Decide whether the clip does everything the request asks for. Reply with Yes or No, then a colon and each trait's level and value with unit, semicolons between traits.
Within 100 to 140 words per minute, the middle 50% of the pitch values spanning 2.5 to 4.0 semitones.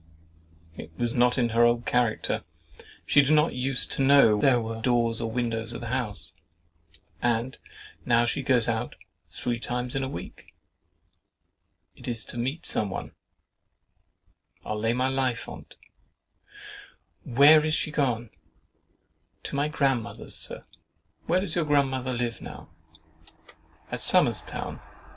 Yes: slow, 135 wpm; average, 2.9 semitones